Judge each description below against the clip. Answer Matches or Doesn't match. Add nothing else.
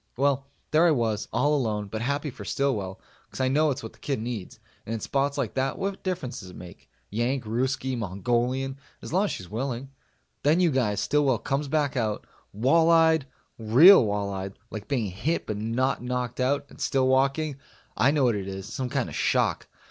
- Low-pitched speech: Matches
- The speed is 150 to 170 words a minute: Doesn't match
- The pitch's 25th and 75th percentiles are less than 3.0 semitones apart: Doesn't match